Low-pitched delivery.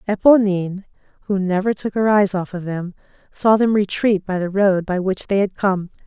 No: high, 195 Hz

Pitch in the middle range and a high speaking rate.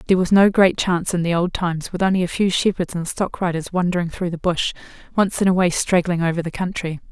Yes: medium, 175 Hz; fast, 245 wpm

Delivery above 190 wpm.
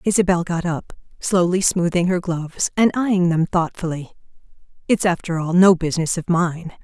No: average, 160 wpm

